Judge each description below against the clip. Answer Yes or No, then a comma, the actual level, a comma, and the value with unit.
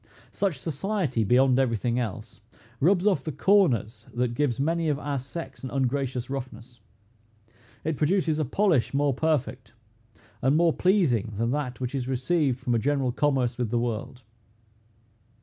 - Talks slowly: No, average, 155 wpm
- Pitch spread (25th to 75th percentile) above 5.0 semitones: No, average, 4.2 semitones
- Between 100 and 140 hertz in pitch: Yes, low, 135 Hz